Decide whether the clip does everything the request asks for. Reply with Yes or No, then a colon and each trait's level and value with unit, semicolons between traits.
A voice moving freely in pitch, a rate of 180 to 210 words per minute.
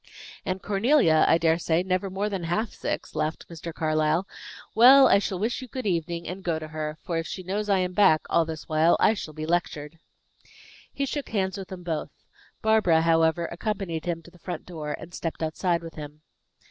No: average, 3.3 semitones; fast, 205 wpm